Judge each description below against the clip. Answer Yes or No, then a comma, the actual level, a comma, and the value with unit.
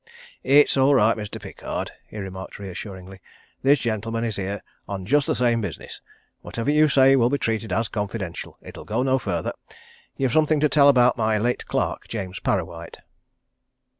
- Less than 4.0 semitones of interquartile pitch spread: No, average, 4.8 semitones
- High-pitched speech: No, low, 115 Hz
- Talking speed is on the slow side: No, average, 165 wpm